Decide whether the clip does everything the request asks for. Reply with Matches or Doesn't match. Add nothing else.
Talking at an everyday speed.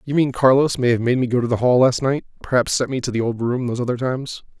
Doesn't match